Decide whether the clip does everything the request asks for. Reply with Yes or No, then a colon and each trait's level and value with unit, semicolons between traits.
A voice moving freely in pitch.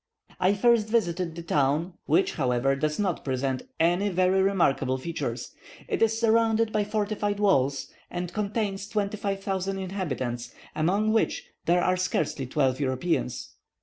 Yes: wide, 6.5 semitones